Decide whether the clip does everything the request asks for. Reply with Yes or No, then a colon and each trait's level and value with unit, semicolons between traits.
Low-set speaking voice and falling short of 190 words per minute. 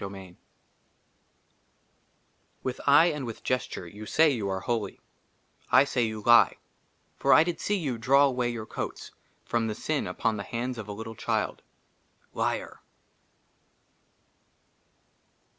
Yes: low, 120 Hz; average, 140 wpm